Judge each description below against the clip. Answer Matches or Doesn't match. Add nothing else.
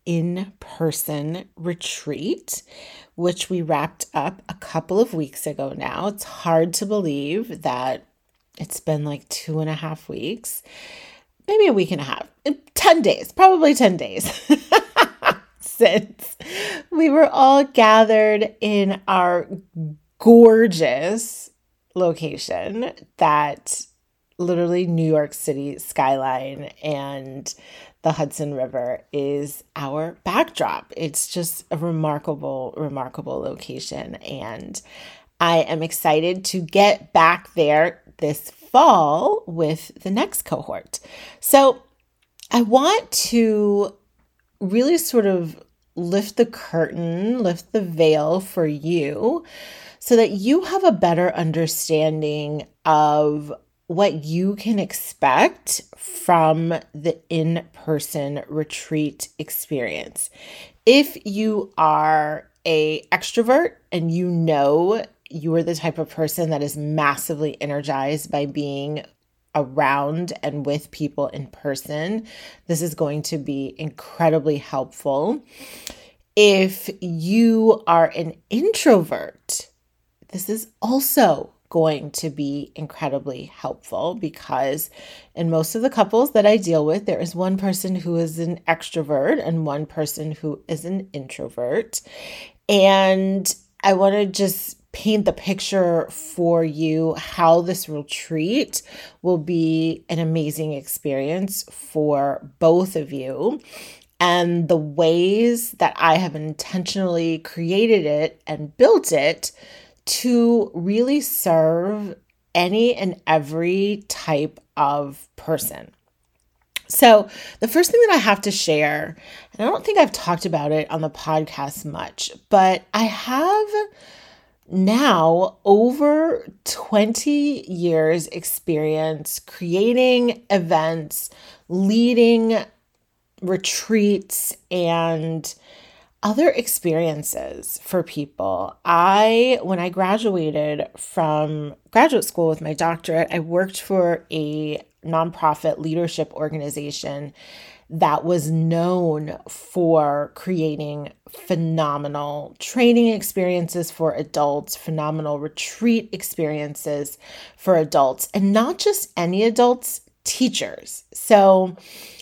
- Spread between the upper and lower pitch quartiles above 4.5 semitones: Matches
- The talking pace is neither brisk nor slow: Doesn't match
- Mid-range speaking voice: Matches